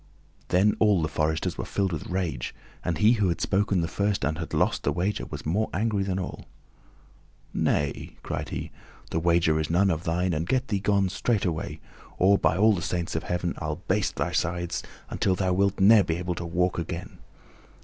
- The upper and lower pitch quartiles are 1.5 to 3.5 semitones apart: Yes, average, 3.1 semitones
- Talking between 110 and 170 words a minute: No, average, 200 wpm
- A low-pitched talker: Yes, very low, 90 Hz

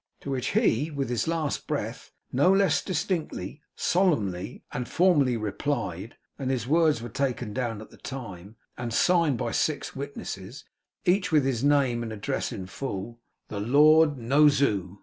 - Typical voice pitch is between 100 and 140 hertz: Yes, low, 135 Hz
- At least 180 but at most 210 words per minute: No, average, 160 wpm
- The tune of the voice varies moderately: Yes, average, 5.0 semitones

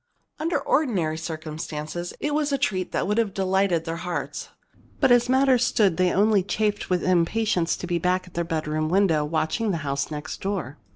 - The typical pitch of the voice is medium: Yes, medium, 180 Hz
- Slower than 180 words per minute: No, average, 185 wpm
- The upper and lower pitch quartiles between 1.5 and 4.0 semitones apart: No, average, 4.8 semitones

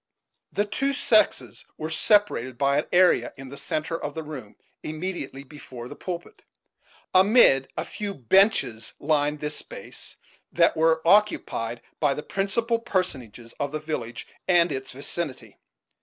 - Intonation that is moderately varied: No, wide, 5.9 semitones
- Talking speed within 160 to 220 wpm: No, average, 140 wpm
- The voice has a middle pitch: Yes, medium, 155 Hz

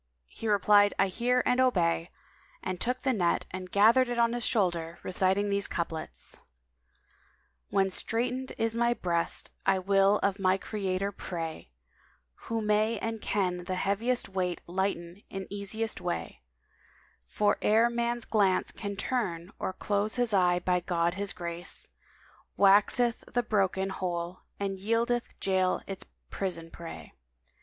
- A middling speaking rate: Yes, average, 145 wpm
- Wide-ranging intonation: No, average, 3.8 semitones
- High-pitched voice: Yes, high, 195 Hz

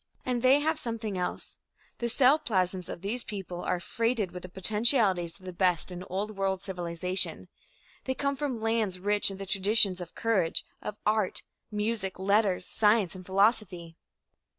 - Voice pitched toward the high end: Yes, high, 200 Hz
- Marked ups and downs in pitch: No, average, 3.7 semitones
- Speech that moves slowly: No, average, 165 wpm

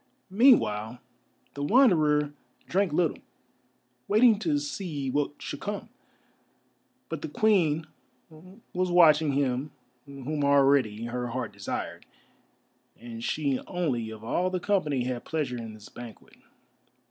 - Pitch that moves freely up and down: Yes, wide, 6.5 semitones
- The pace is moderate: No, slow, 120 wpm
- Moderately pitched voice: Yes, medium, 145 Hz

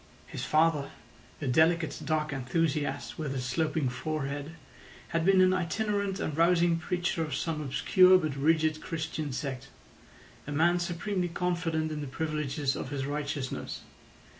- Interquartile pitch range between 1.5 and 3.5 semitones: Yes, average, 2.9 semitones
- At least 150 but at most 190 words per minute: No, average, 140 wpm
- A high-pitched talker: No, medium, 155 Hz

